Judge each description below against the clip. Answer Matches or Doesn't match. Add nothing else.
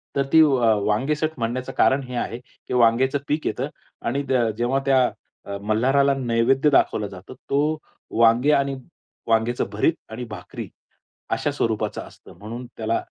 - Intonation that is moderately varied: Matches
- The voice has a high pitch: Doesn't match